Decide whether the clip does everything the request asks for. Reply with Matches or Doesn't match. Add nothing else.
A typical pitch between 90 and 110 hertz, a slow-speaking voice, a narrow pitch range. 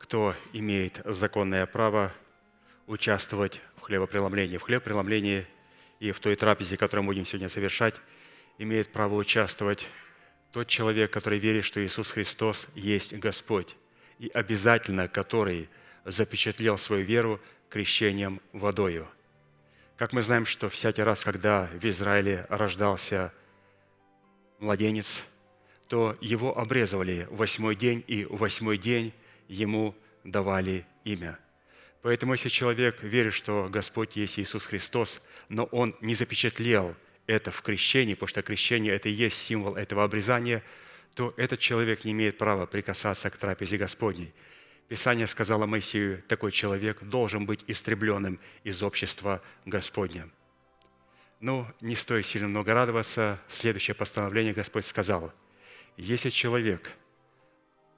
Doesn't match